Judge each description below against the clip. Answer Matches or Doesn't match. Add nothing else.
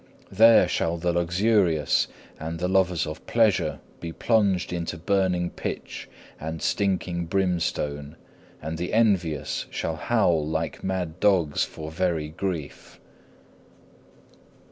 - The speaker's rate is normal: Doesn't match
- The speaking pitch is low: Matches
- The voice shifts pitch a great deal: Doesn't match